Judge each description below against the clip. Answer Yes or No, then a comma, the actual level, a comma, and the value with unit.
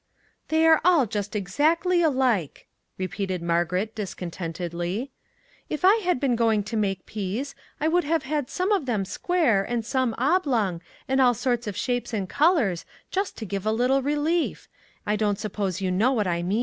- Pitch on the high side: Yes, high, 230 Hz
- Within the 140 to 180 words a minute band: No, average, 190 wpm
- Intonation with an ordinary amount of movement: No, wide, 7.0 semitones